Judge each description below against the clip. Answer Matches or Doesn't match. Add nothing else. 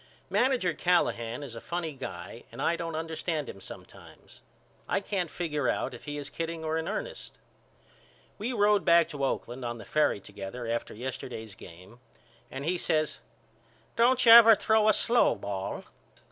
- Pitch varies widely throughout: Matches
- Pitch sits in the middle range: Matches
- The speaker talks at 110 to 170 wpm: Matches